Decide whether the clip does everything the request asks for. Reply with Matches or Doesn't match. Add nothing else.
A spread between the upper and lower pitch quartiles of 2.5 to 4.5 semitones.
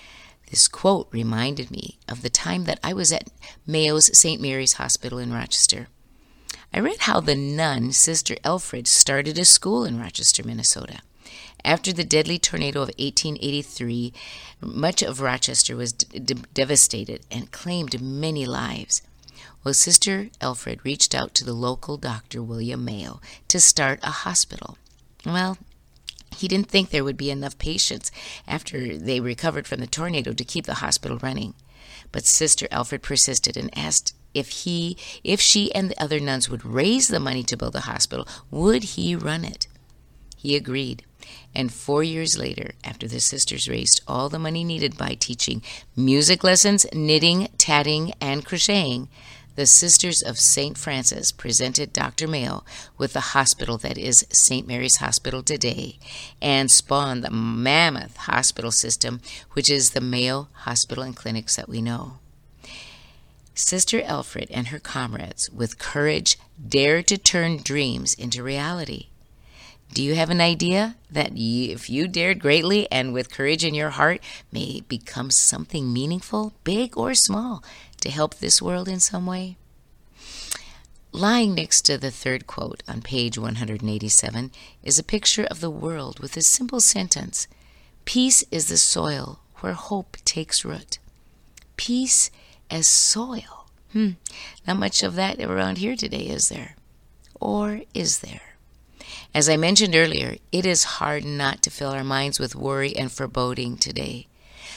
Doesn't match